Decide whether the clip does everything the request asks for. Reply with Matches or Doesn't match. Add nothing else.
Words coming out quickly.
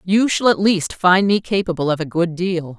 Matches